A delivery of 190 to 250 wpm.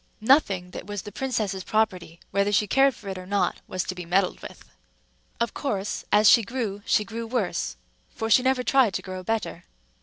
Yes: average, 200 wpm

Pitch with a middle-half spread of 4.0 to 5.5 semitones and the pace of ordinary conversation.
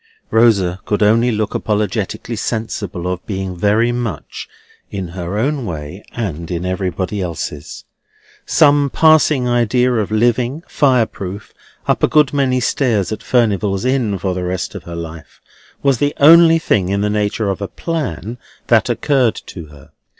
Yes: average, 5.1 semitones; average, 155 wpm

